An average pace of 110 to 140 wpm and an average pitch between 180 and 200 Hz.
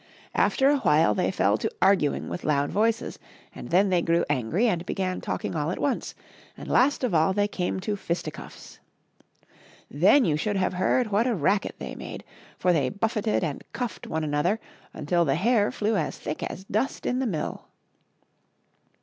No: average, 180 wpm; medium, 185 Hz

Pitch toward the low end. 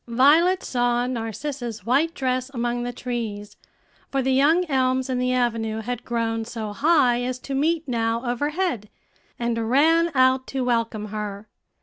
No: high, 245 Hz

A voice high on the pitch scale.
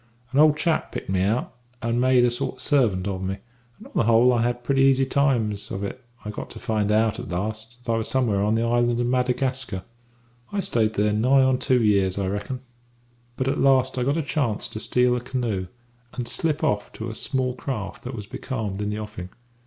No: low, 120 Hz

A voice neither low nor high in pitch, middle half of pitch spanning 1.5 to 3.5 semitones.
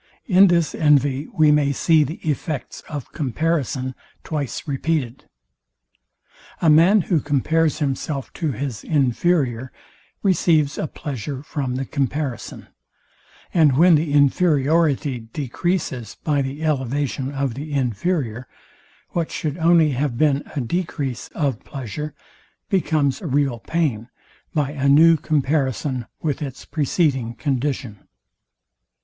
Yes: medium, 145 Hz; average, 3.2 semitones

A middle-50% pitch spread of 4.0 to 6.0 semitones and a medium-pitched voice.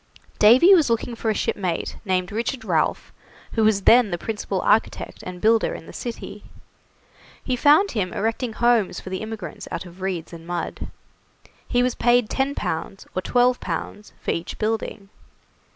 No: average, 4.5 semitones; high, 220 Hz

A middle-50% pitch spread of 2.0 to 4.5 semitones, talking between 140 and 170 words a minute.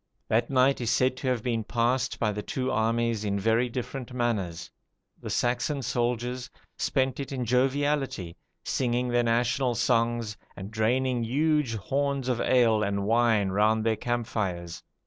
Yes: narrow, 2.5 semitones; average, 155 wpm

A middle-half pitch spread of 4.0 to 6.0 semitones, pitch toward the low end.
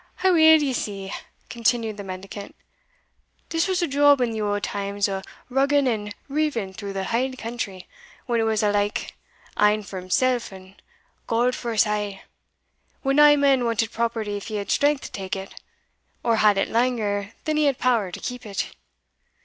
No: average, 4.3 semitones; high, 225 Hz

